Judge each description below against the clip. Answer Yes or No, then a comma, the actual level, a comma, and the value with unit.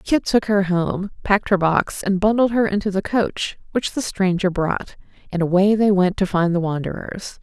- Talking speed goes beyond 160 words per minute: Yes, average, 200 wpm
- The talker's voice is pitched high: Yes, high, 195 Hz